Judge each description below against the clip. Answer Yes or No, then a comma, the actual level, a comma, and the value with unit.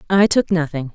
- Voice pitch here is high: No, medium, 170 Hz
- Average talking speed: Yes, average, 190 wpm